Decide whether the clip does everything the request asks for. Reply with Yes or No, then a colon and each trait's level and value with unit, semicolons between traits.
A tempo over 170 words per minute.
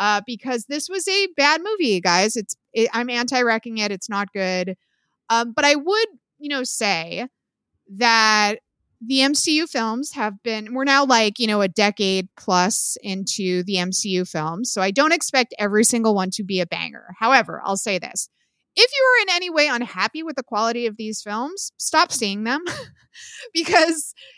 Yes: average, 180 wpm